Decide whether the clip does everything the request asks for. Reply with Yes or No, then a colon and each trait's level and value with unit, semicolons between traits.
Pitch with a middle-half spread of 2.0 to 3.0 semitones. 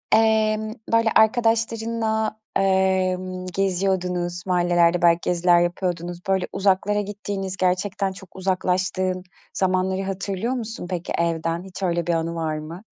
Yes: narrow, 2.6 semitones